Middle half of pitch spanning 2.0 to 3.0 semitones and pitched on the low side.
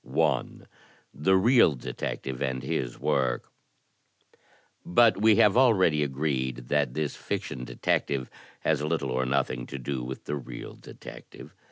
No: average, 4.5 semitones; very low, 70 Hz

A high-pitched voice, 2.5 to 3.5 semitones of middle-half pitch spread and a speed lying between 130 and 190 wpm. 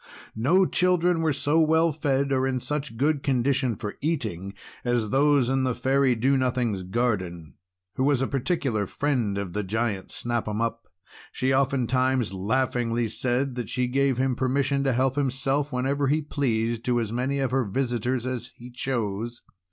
No: low, 130 Hz; average, 2.9 semitones; average, 170 wpm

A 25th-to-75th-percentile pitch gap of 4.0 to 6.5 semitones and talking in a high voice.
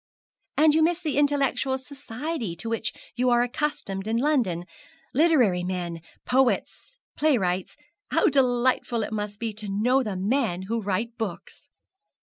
Yes: wide, 5.4 semitones; high, 240 Hz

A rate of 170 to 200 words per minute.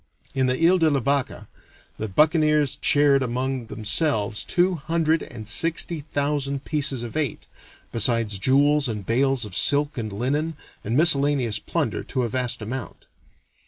No: average, 150 wpm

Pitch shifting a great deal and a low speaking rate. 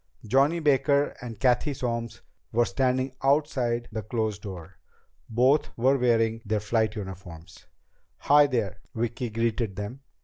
No: average, 3.6 semitones; slow, 130 wpm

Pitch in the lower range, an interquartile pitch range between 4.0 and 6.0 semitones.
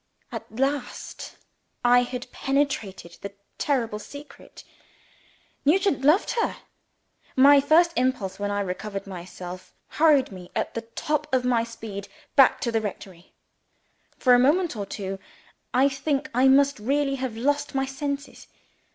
No: very high, 255 Hz; average, 5.3 semitones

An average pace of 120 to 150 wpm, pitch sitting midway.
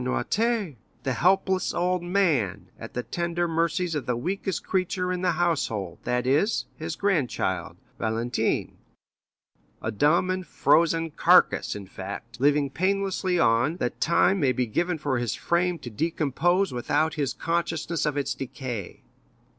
Yes: average, 145 wpm; medium, 160 Hz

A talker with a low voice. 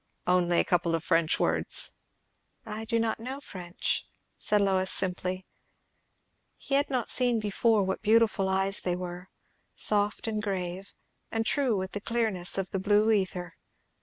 No: high, 195 Hz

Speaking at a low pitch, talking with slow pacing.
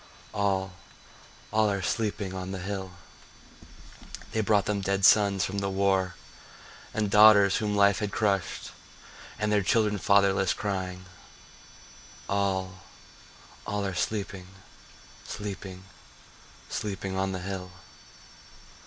Yes: low, 100 Hz; slow, 115 wpm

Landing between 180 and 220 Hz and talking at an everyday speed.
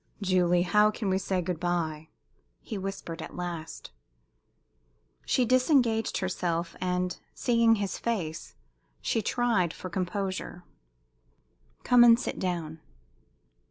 No: medium, 185 Hz; slow, 115 wpm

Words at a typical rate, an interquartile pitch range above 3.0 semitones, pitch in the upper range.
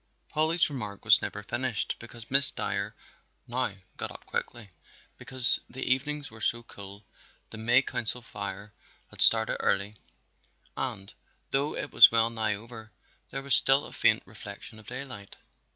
No: average, 150 wpm; average, 4.0 semitones; low, 115 Hz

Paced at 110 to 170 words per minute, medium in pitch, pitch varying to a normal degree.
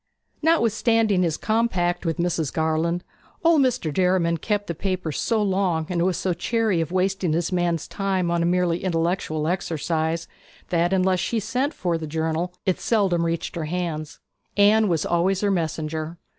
Yes: average, 165 wpm; medium, 175 Hz; average, 3.0 semitones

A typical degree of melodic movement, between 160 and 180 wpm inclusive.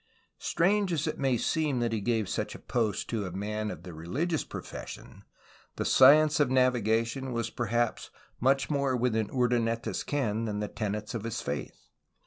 Yes: average, 4.0 semitones; average, 175 wpm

